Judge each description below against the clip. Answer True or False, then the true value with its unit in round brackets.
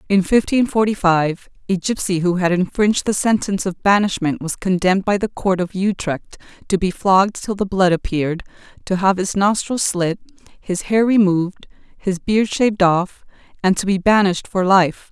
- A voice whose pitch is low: False (190 Hz)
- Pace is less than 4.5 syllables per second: False (5.1 syllables/s)